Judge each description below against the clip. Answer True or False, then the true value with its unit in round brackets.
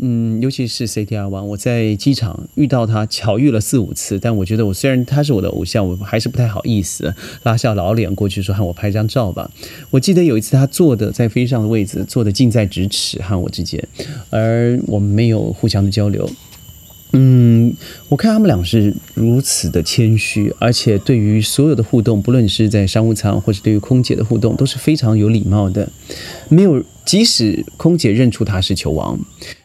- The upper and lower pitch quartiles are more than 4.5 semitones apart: False (3.6 semitones)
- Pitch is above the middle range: False (110 Hz)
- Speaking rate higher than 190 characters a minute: True (300 characters per minute)